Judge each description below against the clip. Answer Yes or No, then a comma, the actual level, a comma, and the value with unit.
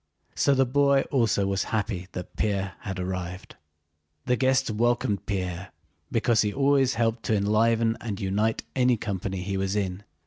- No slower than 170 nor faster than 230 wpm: No, average, 160 wpm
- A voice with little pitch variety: No, average, 3.8 semitones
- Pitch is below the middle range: Yes, low, 105 Hz